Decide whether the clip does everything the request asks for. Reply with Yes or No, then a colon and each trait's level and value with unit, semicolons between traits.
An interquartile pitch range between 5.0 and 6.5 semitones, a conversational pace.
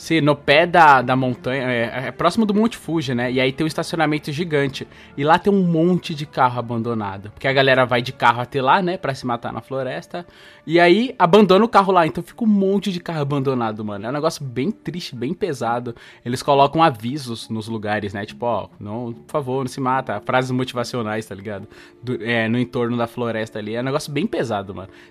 No: wide, 5.6 semitones; fast, 220 wpm